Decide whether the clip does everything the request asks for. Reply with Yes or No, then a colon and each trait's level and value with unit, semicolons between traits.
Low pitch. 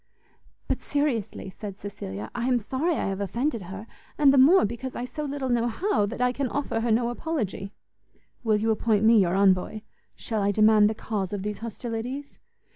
No: high, 225 Hz